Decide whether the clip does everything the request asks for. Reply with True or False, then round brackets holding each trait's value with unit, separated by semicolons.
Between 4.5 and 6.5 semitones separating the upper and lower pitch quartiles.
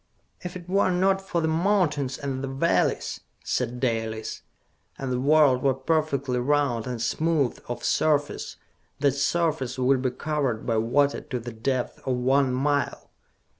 False (3.7 semitones)